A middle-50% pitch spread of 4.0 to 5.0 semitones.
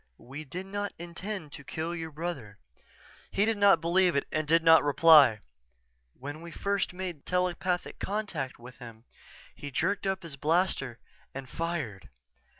Yes: average, 4.7 semitones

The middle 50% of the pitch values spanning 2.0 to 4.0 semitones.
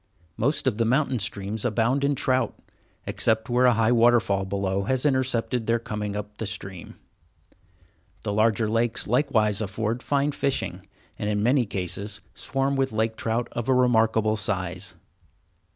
Yes: average, 3.3 semitones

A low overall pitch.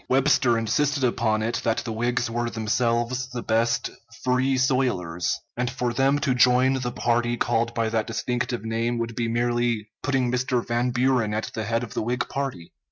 Yes: low, 120 Hz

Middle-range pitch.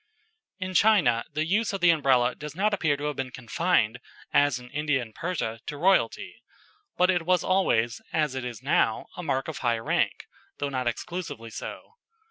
Yes: medium, 150 Hz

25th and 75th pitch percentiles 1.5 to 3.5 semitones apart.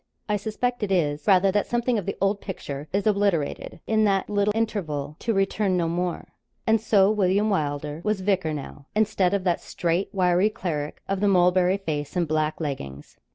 No: average, 4.3 semitones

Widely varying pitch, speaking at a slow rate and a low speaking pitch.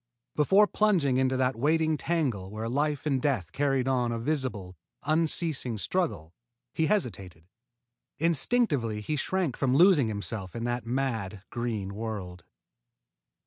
Yes: wide, 6.0 semitones; slow, 130 wpm; low, 130 Hz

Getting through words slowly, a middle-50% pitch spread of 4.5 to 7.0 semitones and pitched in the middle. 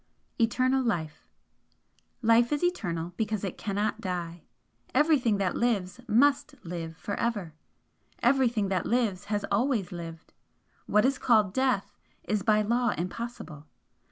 No: slow, 130 wpm; average, 5.0 semitones; high, 215 Hz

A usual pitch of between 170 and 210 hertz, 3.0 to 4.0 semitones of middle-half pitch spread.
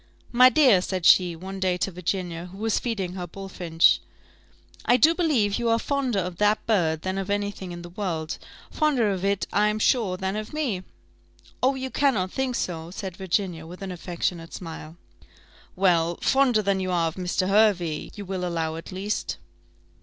Yes: high, 190 Hz; average, 3.5 semitones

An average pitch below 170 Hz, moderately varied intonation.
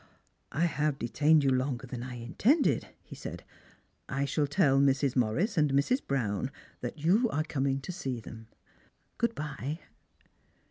Yes: medium, 140 Hz; average, 3.2 semitones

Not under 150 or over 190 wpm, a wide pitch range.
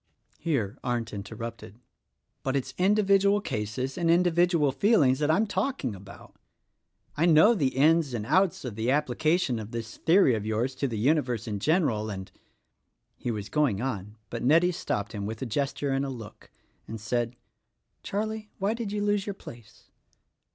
Yes: average, 180 wpm; wide, 7.6 semitones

